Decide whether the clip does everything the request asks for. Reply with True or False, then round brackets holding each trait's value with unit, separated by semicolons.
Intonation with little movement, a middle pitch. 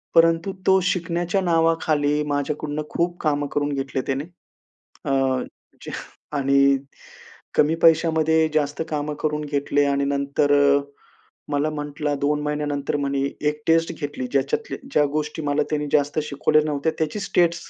True (2.2 semitones; 150 Hz)